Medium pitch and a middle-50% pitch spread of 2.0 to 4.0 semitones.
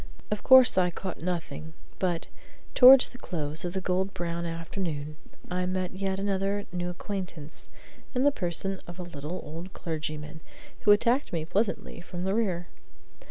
Yes: medium, 180 Hz; average, 2.8 semitones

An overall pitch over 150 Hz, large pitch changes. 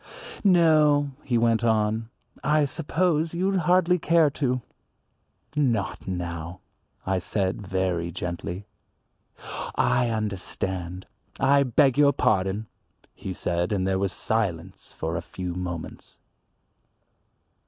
No: low, 110 Hz; wide, 7.8 semitones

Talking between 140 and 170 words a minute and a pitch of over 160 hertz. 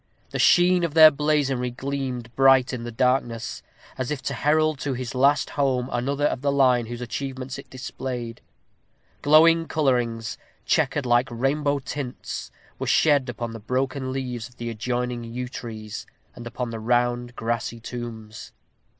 No: average, 155 wpm; low, 125 Hz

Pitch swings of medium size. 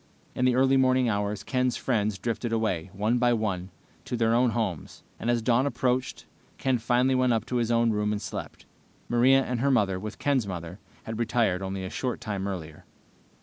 Yes: average, 3.7 semitones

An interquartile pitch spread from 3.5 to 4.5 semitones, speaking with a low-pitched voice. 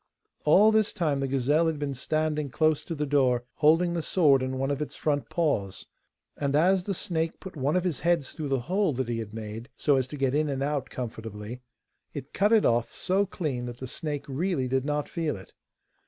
No: average, 4.0 semitones; medium, 145 Hz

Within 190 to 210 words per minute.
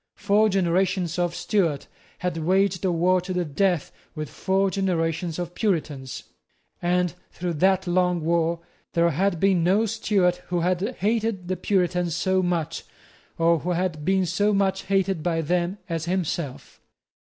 No: average, 155 wpm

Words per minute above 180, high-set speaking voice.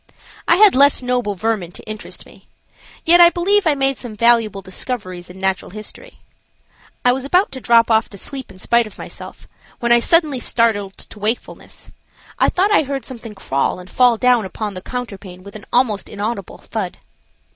Yes: average, 190 wpm; high, 230 Hz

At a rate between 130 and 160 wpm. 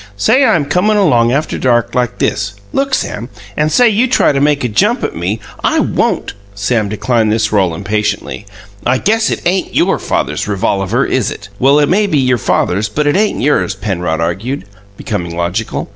No: average, 190 wpm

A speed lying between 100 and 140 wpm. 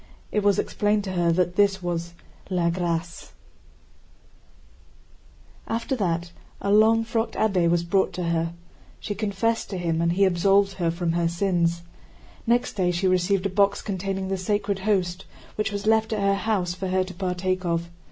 No: average, 170 wpm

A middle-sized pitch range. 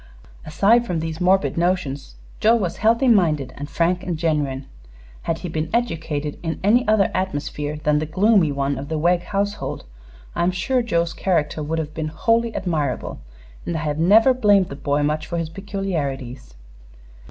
Yes: average, 4.6 semitones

